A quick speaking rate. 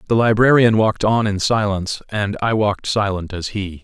No: average, 190 wpm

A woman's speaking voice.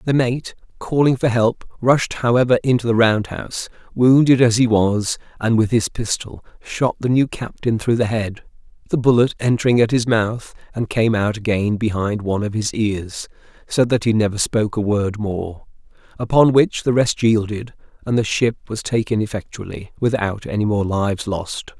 No: male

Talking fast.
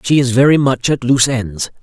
Yes: fast, 230 wpm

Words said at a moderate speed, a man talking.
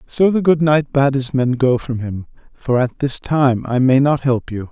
No: fast, 240 wpm; male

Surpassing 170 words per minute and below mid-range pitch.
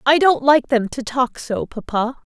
No: fast, 205 wpm; very high, 250 Hz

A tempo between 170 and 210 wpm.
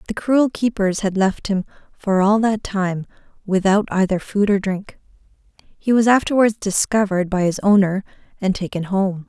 No: average, 160 wpm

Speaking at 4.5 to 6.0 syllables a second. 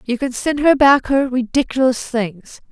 No: 4.3 syllables/s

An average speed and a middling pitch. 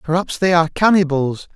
Yes: average, 155 wpm; medium, 165 Hz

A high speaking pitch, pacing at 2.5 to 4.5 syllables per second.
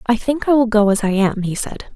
No: high, 220 Hz; 5.6 syllables/s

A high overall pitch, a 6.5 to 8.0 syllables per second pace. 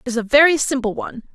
Yes: very high, 260 Hz; 7.0 syllables/s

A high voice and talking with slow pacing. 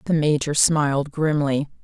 No: medium, 145 Hz; slow, 130 wpm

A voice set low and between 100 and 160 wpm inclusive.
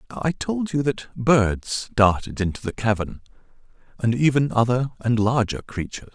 Yes: low, 120 Hz; average, 145 wpm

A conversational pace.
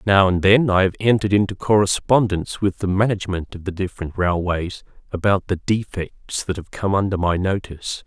Yes: average, 180 wpm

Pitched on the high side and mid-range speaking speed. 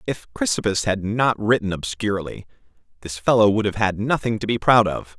No: low, 105 Hz; average, 185 wpm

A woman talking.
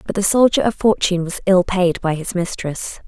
Yes: female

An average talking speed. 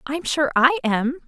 Yes: average, 190 wpm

